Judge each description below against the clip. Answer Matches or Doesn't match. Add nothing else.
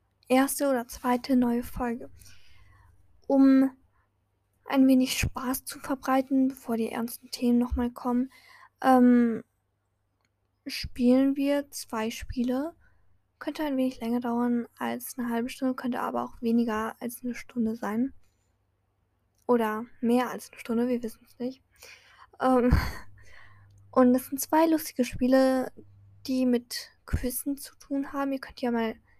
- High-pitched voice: Matches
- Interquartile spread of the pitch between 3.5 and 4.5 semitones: Doesn't match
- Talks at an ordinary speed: Matches